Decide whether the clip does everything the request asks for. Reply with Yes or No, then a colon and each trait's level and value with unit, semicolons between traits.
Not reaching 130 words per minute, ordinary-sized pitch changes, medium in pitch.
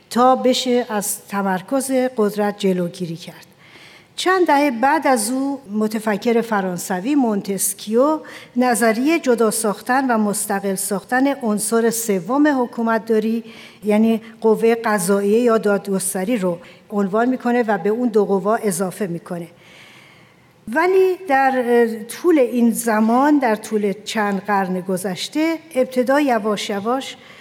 No: average, 115 wpm; average, 3.9 semitones; high, 225 Hz